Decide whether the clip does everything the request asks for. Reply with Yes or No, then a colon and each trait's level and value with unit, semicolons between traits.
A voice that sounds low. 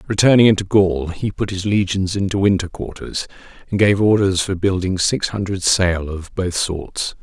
Yes: very low, 95 Hz